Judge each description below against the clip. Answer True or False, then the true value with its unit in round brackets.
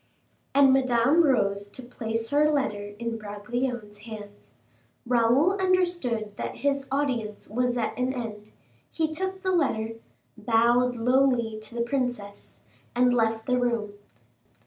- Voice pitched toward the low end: False (240 Hz)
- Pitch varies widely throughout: False (3.6 semitones)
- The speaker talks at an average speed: False (130 wpm)